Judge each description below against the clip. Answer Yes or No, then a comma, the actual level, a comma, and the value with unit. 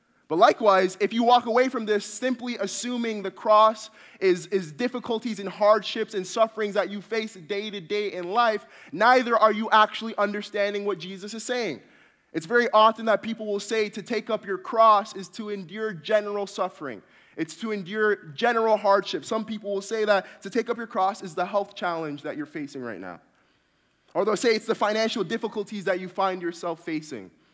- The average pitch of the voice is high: Yes, high, 215 Hz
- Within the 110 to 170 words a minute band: No, average, 195 wpm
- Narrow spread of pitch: Yes, narrow, 2.3 semitones